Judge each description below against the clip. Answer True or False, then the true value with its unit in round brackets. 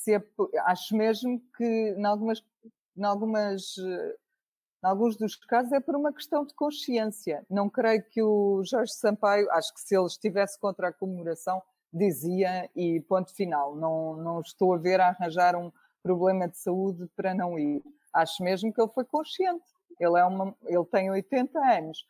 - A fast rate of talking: False (170 wpm)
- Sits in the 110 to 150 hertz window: False (200 Hz)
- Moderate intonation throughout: True (4.0 semitones)